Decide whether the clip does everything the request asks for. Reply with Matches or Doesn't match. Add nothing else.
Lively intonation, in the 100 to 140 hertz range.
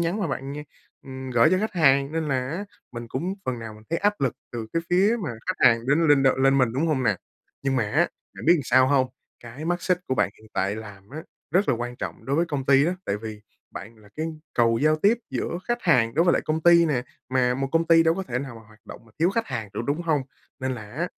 Matches